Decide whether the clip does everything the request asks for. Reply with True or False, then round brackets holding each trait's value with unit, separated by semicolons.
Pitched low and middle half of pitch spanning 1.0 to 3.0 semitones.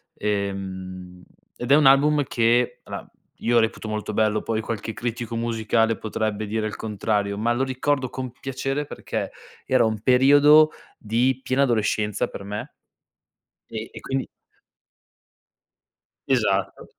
False (115 Hz; 3.5 semitones)